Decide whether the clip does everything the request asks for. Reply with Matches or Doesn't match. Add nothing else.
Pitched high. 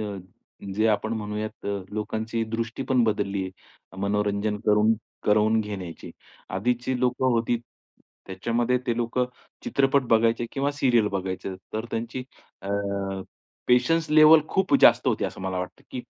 Doesn't match